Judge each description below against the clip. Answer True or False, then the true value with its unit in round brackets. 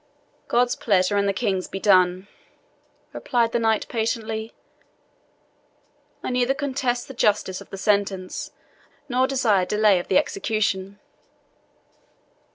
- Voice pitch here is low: False (215 Hz)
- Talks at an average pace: False (120 wpm)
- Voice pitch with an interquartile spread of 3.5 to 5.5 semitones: True (3.8 semitones)